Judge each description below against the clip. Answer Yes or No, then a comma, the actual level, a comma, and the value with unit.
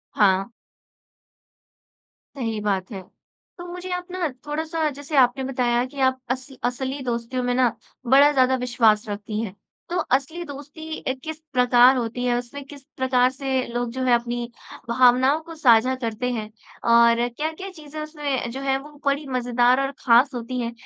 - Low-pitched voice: No, very high, 255 Hz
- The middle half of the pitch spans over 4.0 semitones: No, average, 3.0 semitones